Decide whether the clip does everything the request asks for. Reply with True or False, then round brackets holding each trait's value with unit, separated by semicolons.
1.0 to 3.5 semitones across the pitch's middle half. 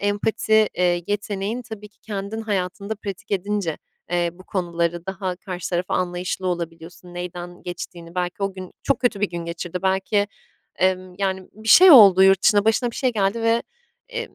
True (2.8 semitones)